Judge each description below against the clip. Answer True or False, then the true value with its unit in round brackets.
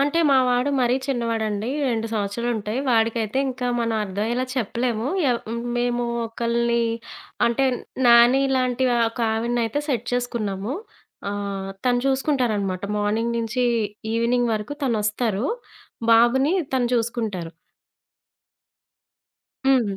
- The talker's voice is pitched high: True (235 Hz)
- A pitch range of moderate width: False (2.3 semitones)